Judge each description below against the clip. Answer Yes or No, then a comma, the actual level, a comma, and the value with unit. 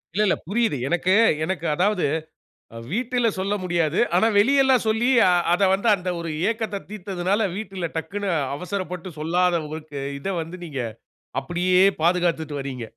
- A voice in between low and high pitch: Yes, medium, 180 Hz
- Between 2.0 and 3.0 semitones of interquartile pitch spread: No, average, 3.6 semitones